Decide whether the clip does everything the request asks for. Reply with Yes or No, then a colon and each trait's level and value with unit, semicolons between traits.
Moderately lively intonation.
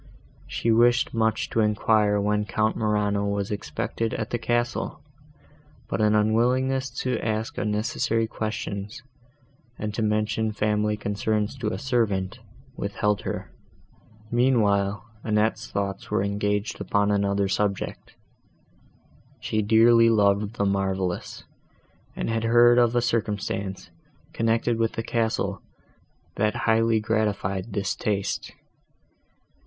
No: narrow, 1.9 semitones